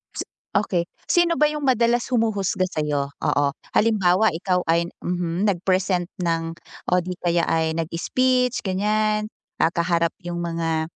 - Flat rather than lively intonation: No, average, 4.2 semitones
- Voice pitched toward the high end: No, medium, 180 Hz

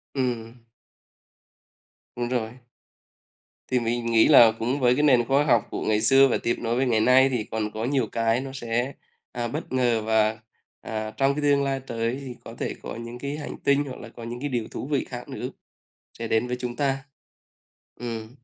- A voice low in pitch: Yes, low, 120 Hz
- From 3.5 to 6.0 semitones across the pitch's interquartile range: No, average, 2.7 semitones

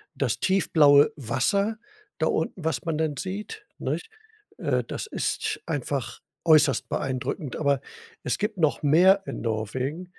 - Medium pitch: Yes, medium, 155 Hz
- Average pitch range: No, wide, 5.9 semitones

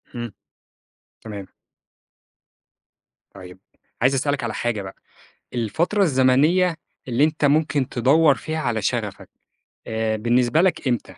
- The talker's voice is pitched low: Yes, low, 130 Hz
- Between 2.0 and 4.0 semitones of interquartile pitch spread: No, average, 5.3 semitones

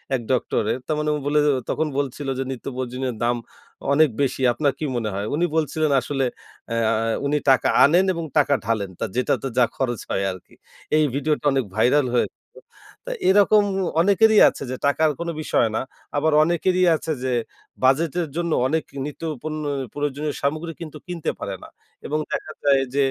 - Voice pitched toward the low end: No, medium, 145 Hz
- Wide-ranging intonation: No, average, 3.5 semitones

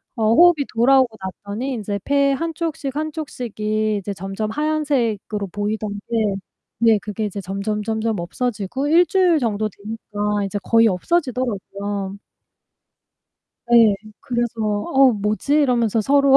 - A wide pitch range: No, average, 4.8 semitones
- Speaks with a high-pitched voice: Yes, high, 225 Hz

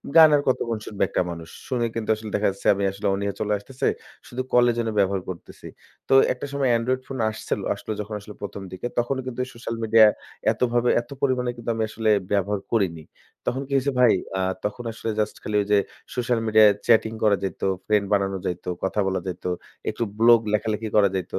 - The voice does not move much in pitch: No, average, 3.2 semitones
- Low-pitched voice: Yes, low, 110 Hz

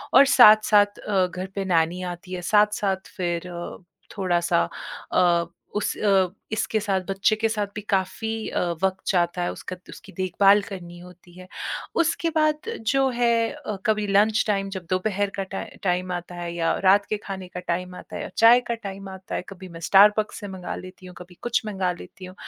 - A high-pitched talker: Yes, high, 195 Hz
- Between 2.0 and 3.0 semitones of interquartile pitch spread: Yes, average, 2.7 semitones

